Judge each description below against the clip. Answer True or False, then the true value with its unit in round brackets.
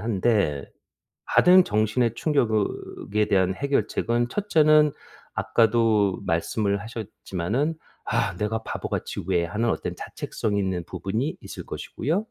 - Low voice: True (110 Hz)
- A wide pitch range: False (4.0 semitones)